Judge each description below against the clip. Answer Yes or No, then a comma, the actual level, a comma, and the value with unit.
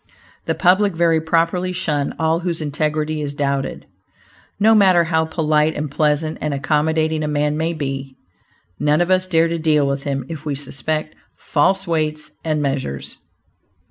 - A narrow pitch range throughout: Yes, narrow, 2.1 semitones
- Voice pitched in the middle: Yes, medium, 155 Hz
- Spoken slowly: No, average, 160 wpm